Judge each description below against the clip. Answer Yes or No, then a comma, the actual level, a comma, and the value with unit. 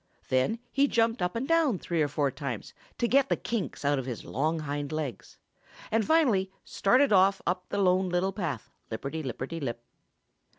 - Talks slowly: No, average, 180 wpm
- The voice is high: No, medium, 180 Hz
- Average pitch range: No, wide, 7.8 semitones